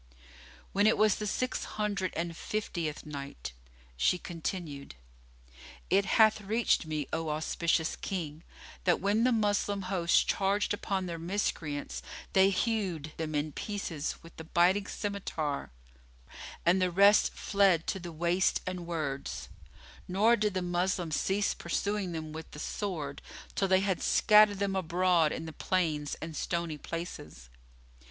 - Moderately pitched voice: Yes, medium, 180 Hz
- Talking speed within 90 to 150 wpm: Yes, average, 145 wpm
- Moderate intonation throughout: Yes, average, 4.0 semitones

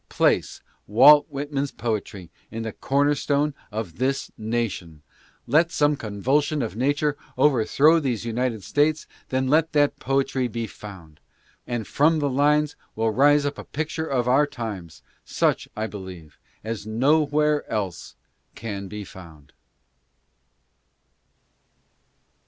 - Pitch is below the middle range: Yes, low, 130 Hz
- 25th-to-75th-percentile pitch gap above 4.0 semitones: Yes, average, 5.3 semitones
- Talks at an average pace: No, slow, 130 wpm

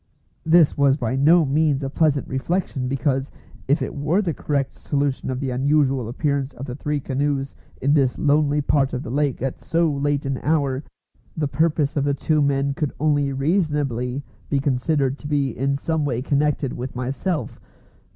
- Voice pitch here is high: No, medium, 140 Hz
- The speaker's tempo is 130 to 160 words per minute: No, average, 180 wpm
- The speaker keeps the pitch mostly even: Yes, narrow, 1.9 semitones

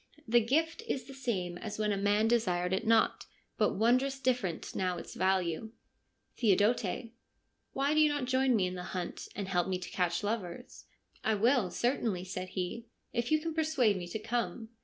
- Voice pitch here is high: Yes, high, 220 Hz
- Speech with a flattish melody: No, average, 5.3 semitones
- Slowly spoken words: No, average, 200 wpm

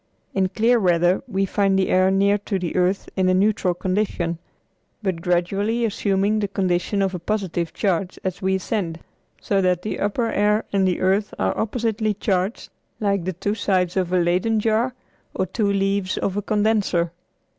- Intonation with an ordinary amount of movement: No, narrow, 2.3 semitones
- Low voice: No, high, 195 Hz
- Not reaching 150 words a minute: No, average, 175 wpm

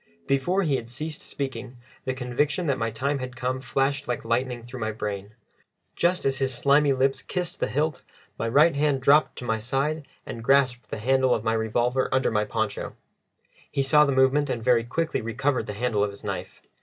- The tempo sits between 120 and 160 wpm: No, average, 200 wpm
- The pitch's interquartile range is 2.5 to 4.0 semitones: Yes, average, 3.3 semitones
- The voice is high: No, low, 130 Hz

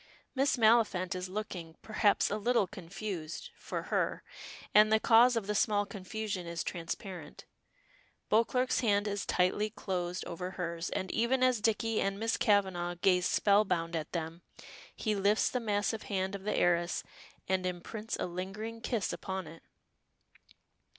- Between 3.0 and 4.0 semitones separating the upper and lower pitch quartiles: Yes, average, 3.3 semitones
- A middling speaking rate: Yes, average, 150 wpm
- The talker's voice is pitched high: Yes, high, 200 Hz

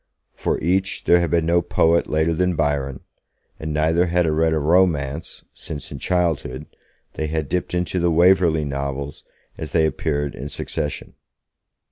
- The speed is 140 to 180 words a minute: Yes, average, 155 wpm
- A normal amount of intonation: Yes, average, 3.0 semitones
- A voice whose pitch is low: Yes, very low, 80 Hz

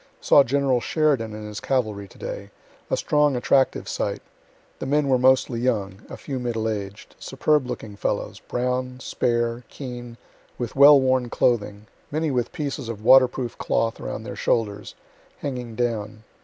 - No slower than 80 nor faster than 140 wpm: No, average, 155 wpm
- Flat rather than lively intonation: No, average, 3.1 semitones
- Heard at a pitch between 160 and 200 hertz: No, low, 125 Hz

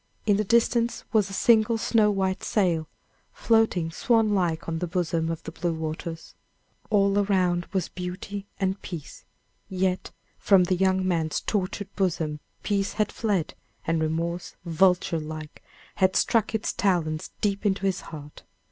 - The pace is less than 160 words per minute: Yes, average, 150 wpm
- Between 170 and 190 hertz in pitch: Yes, medium, 185 Hz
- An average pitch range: Yes, average, 3.5 semitones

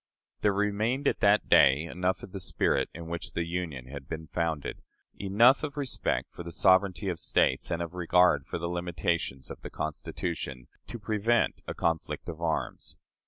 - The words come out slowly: No, average, 175 wpm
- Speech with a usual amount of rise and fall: Yes, average, 3.7 semitones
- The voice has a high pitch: No, very low, 85 Hz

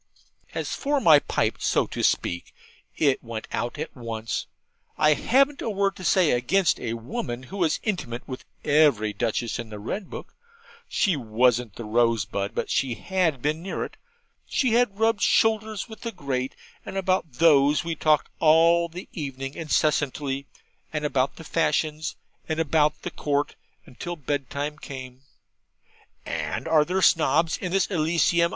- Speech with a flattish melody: No, wide, 5.6 semitones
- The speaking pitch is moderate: Yes, medium, 150 Hz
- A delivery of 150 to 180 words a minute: Yes, average, 160 wpm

